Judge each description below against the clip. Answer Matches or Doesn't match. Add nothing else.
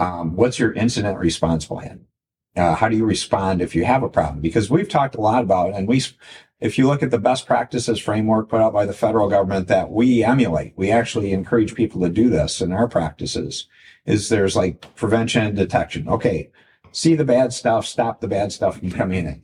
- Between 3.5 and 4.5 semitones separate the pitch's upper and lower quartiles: Matches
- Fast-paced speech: Matches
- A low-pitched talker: Matches